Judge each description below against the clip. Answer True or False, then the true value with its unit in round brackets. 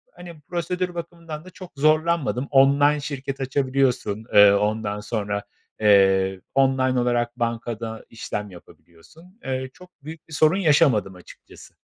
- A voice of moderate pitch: False (130 Hz)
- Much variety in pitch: True (6.4 semitones)